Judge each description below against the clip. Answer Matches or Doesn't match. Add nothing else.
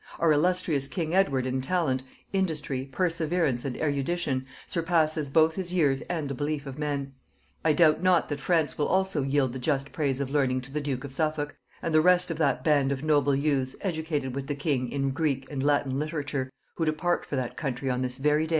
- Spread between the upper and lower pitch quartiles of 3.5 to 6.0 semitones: Doesn't match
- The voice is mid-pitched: Matches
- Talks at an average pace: Doesn't match